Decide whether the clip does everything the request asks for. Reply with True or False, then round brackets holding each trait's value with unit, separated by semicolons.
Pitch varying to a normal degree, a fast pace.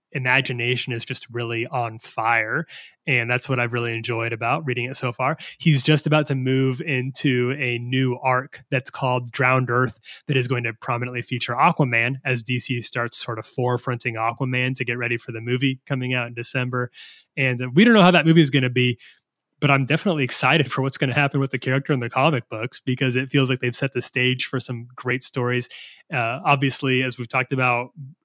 False (1.8 semitones; 210 wpm)